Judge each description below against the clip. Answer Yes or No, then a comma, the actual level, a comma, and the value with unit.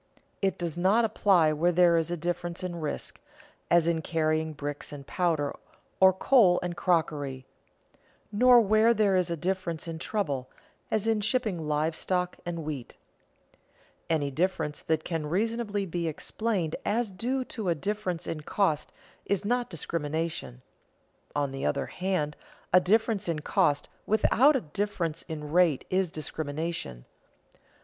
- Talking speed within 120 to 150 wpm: Yes, average, 145 wpm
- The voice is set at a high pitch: No, medium, 175 Hz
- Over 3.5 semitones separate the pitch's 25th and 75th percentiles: Yes, average, 4.3 semitones